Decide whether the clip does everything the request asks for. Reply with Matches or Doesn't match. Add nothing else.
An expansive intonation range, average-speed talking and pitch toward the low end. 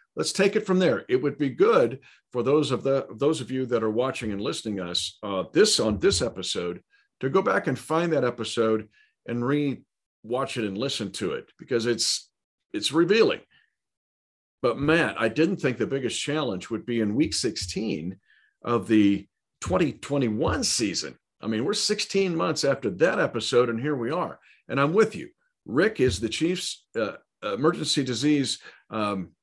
Matches